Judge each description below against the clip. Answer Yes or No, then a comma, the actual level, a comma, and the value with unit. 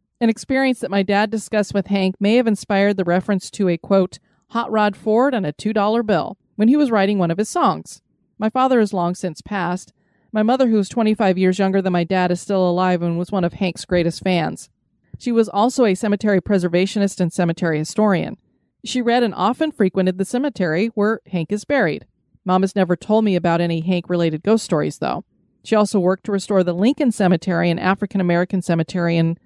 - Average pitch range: Yes, average, 3.3 semitones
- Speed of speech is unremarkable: No, fast, 210 wpm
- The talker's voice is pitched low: No, high, 195 Hz